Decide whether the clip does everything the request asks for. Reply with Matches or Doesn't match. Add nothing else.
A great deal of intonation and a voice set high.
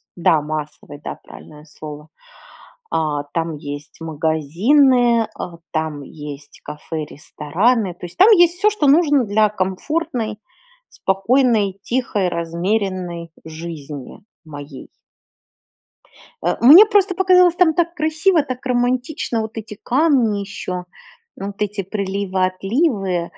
Matches